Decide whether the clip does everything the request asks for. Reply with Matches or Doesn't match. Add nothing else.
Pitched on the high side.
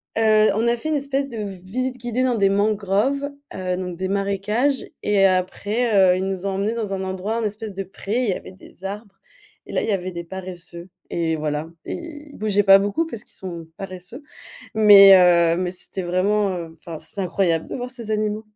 Matches